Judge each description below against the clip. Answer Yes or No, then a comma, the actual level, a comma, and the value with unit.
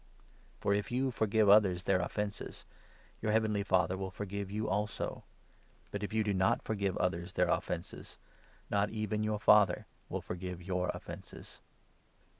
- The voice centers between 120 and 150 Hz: No, low, 100 Hz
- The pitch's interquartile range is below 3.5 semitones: Yes, narrow, 2.4 semitones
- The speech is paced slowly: No, average, 160 wpm